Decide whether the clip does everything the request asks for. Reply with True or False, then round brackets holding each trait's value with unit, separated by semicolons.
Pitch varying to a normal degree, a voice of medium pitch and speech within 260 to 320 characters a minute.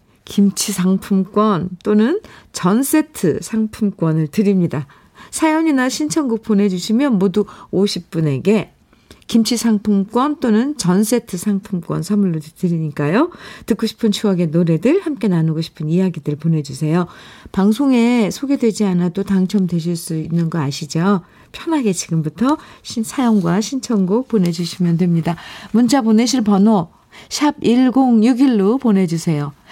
False (5.0 semitones; 205 Hz; 280 characters per minute)